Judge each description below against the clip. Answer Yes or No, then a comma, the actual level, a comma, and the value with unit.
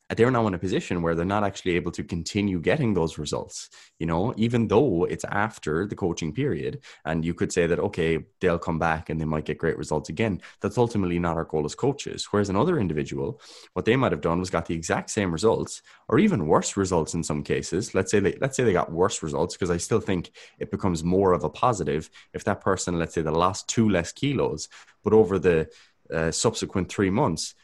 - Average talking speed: No, fast, 230 wpm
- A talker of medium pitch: No, very low, 90 Hz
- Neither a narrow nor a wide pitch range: Yes, average, 3.5 semitones